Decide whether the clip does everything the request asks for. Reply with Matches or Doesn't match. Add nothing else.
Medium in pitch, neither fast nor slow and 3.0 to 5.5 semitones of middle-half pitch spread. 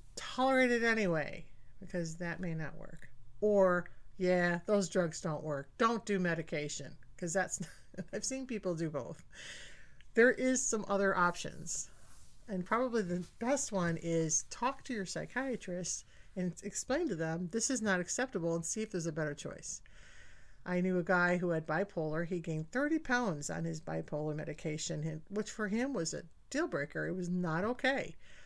Matches